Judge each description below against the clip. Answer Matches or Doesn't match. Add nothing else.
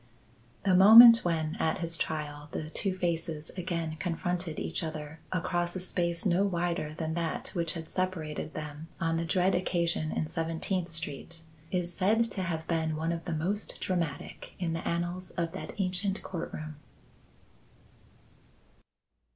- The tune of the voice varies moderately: Doesn't match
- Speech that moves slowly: Doesn't match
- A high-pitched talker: Doesn't match